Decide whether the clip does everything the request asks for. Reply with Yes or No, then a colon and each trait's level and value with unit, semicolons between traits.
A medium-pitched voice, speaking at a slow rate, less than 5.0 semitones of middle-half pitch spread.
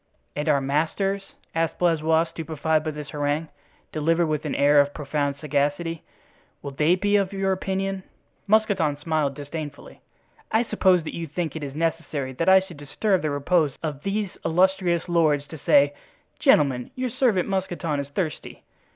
No: medium, 160 Hz; average, 160 wpm; average, 4.4 semitones